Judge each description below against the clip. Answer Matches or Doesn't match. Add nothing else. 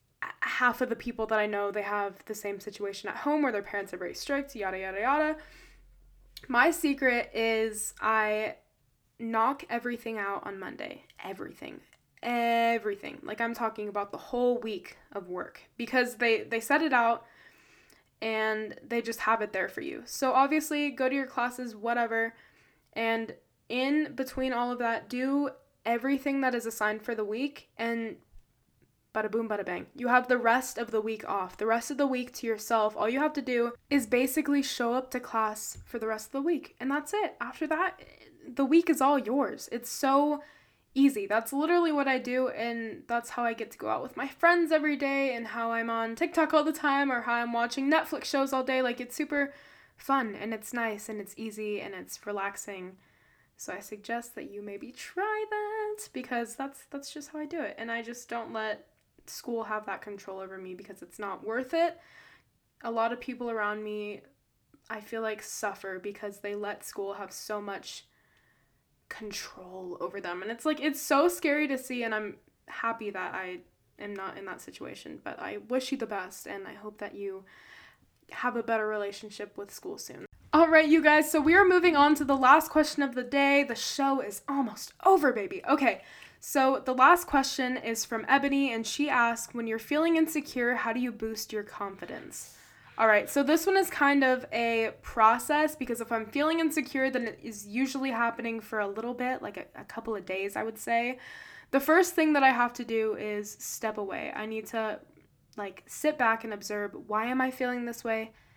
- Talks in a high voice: Matches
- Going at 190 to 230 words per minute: Matches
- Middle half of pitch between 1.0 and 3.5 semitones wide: Doesn't match